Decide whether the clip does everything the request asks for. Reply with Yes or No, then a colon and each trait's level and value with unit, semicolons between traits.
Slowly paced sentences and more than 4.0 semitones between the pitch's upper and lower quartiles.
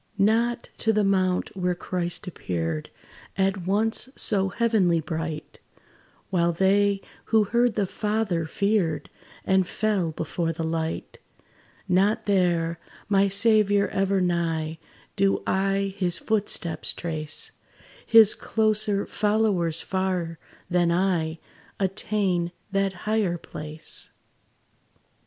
No: slow, 105 wpm; average, 3.3 semitones